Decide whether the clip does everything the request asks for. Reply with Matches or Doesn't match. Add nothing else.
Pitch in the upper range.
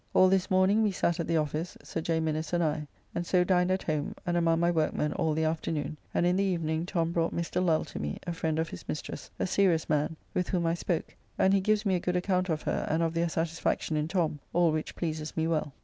Doesn't match